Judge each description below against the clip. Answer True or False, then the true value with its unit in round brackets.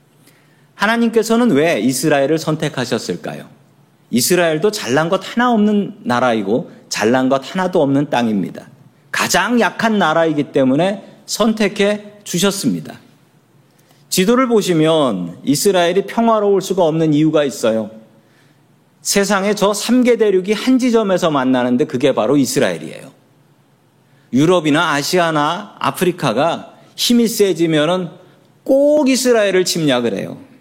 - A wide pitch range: True (6.2 semitones)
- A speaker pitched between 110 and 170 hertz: False (180 Hz)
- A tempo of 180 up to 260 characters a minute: False (290 characters per minute)